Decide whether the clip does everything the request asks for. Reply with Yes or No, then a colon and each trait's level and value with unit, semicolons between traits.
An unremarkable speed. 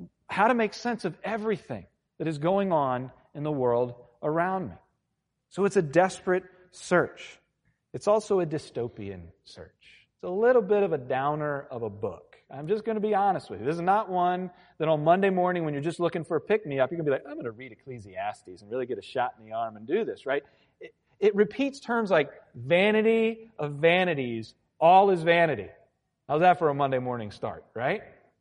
No: fast, 215 wpm